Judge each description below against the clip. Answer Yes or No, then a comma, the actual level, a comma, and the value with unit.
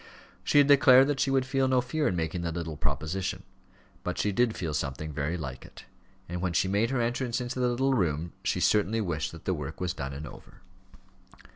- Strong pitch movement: Yes, wide, 8.0 semitones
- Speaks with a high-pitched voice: No, very low, 95 Hz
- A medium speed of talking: No, fast, 220 wpm